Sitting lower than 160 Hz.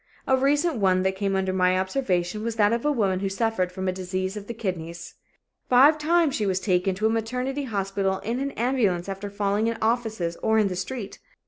No: high, 205 Hz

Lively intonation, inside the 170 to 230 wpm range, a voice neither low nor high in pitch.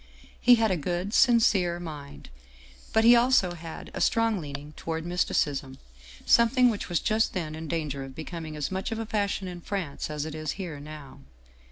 Yes: wide, 5.8 semitones; average, 185 wpm; medium, 175 Hz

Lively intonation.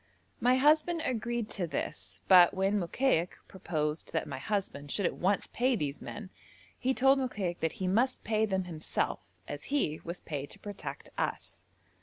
Yes: wide, 7.1 semitones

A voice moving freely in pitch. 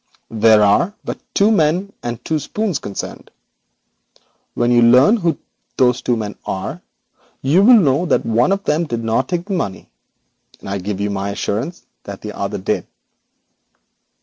Yes: wide, 8.1 semitones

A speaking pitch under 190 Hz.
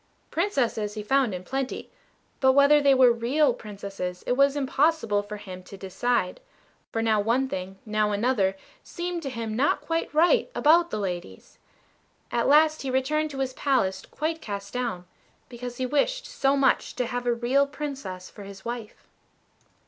No: very high, 250 Hz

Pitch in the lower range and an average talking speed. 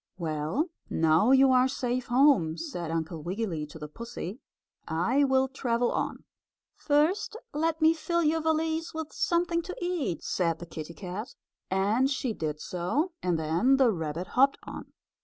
No: high, 245 Hz; average, 160 wpm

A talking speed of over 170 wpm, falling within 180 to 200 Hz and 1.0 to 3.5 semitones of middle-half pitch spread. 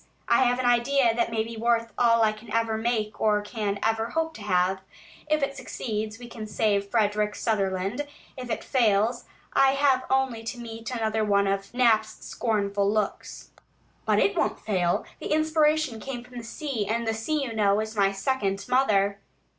No: average, 180 wpm; high, 225 Hz; average, 3.0 semitones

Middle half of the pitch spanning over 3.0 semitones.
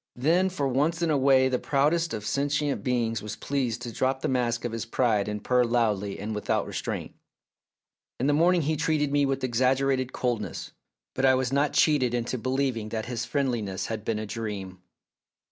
Yes: average, 3.7 semitones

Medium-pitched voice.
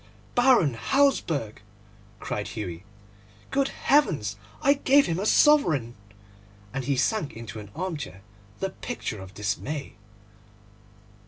Yes: medium, 150 Hz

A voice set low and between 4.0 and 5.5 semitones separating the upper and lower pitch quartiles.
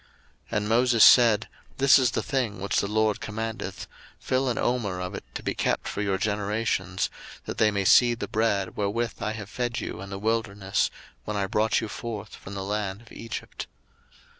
No: low, 105 Hz; narrow, 2.6 semitones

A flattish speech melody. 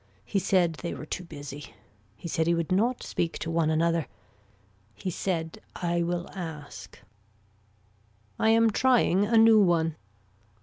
No: average, 3.3 semitones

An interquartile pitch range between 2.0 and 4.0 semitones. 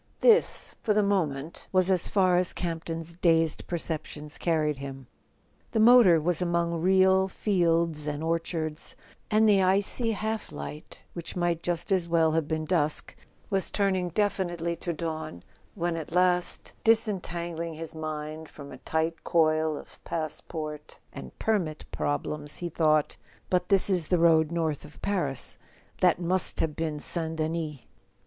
Yes: average, 2.7 semitones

